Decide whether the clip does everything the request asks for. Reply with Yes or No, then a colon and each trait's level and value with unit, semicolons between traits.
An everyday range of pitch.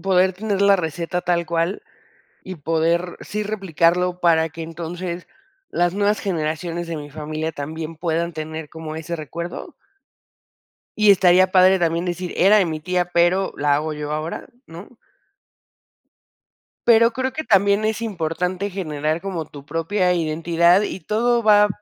Yes: average, 3.1 semitones